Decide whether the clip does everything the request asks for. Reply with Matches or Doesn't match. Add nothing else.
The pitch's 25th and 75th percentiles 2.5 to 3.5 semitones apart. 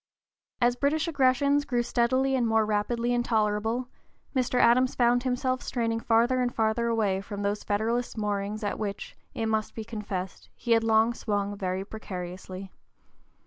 Matches